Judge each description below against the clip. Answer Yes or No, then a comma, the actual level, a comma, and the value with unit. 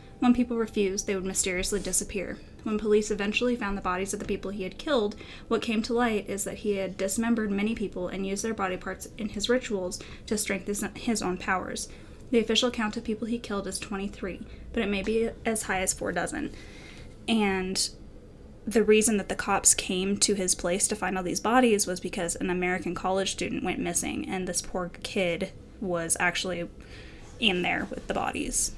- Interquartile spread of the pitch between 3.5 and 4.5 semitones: No, average, 2.8 semitones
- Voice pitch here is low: No, high, 200 Hz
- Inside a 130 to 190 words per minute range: No, average, 200 wpm